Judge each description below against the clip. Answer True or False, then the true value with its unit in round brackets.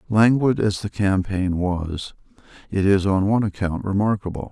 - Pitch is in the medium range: False (100 Hz)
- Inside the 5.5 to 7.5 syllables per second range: False (4.8 syllables/s)